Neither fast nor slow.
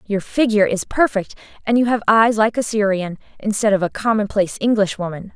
Yes: average, 190 wpm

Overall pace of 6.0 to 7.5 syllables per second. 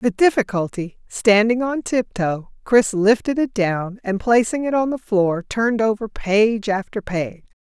No: 4.2 syllables/s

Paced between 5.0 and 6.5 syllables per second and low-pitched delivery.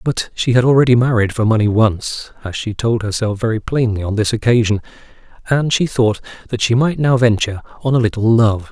Yes: 5.6 syllables/s; low, 115 Hz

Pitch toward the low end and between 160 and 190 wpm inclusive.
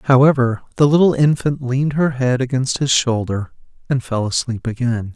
Yes: low, 130 Hz; average, 165 wpm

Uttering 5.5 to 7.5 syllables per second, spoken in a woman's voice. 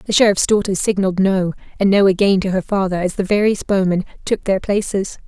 Yes: 5.9 syllables/s; female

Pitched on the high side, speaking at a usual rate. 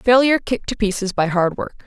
No: high, 215 Hz; fast, 225 wpm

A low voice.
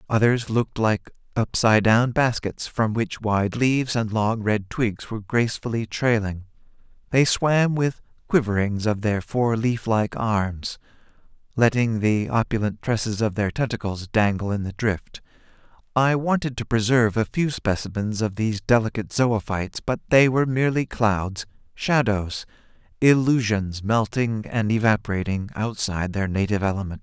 Yes: low, 110 Hz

